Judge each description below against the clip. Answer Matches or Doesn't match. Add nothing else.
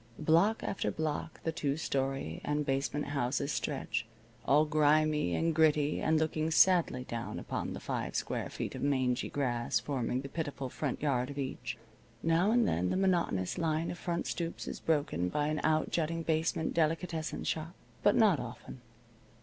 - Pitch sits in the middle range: Matches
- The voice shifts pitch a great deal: Doesn't match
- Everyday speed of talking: Matches